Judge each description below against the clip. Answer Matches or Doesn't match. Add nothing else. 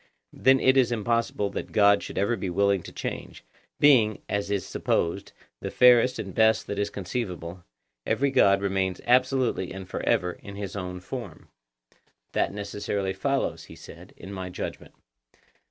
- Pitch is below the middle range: Matches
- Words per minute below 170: Matches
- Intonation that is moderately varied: Matches